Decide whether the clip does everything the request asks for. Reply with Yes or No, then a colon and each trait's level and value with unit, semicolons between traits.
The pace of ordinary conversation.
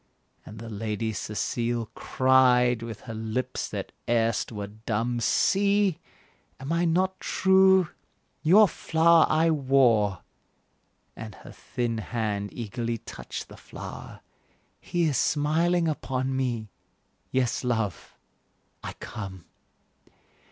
No: slow, 110 wpm